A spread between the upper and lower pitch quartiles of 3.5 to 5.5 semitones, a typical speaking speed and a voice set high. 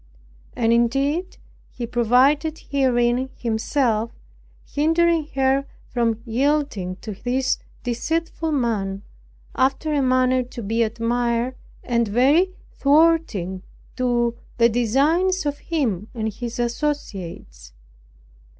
No: average, 4.0 semitones; slow, 100 wpm; high, 245 Hz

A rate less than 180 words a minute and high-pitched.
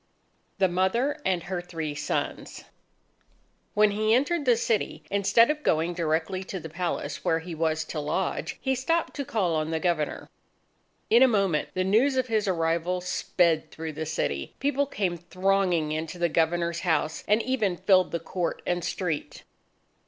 No: average, 165 wpm; medium, 180 Hz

